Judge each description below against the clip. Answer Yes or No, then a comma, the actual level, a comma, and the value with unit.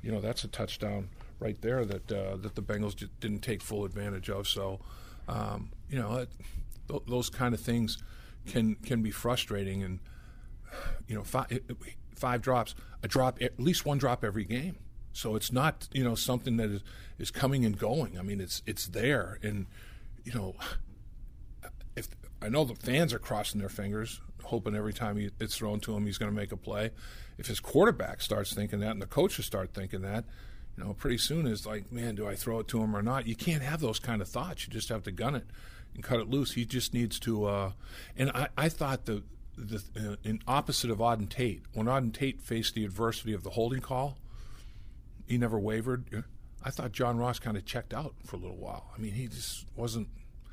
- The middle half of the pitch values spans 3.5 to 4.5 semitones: No, average, 2.9 semitones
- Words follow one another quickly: Yes, fast, 210 wpm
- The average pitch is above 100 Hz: Yes, low, 110 Hz